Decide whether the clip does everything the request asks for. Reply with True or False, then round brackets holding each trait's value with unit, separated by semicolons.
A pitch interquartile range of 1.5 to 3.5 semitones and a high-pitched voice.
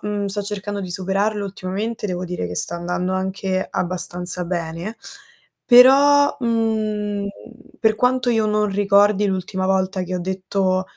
True (2.4 semitones; 195 Hz)